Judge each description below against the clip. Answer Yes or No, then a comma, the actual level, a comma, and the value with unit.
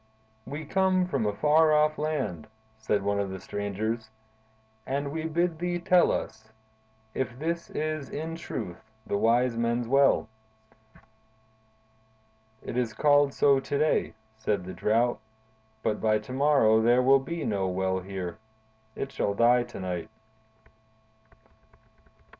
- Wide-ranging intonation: Yes, wide, 6.0 semitones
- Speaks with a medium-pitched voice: No, low, 125 Hz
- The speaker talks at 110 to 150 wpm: Yes, slow, 135 wpm